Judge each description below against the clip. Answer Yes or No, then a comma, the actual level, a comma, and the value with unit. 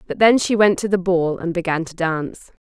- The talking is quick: Yes, fast, 250 wpm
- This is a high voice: No, medium, 180 Hz